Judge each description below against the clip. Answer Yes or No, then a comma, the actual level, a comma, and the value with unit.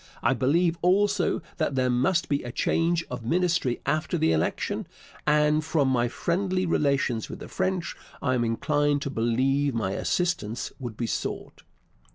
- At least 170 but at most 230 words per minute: No, average, 160 wpm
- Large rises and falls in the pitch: Yes, wide, 5.7 semitones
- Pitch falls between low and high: Yes, medium, 145 Hz